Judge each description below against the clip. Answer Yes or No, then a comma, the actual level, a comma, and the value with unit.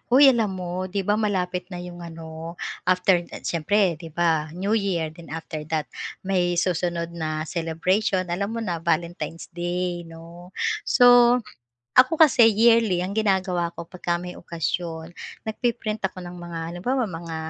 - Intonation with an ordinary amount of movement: Yes, average, 3.1 semitones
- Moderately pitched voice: Yes, medium, 180 Hz